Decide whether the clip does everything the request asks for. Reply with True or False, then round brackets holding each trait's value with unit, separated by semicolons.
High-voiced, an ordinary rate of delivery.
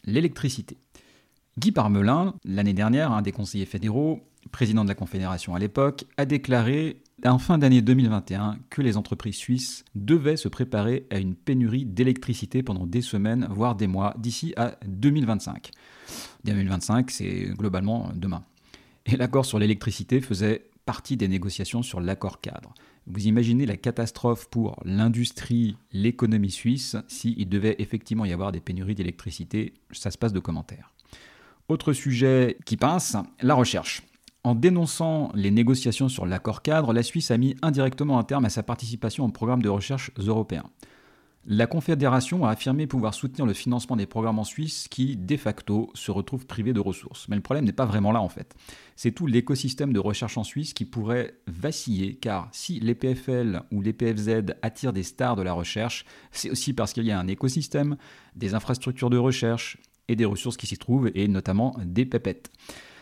False (115 Hz; 170 wpm)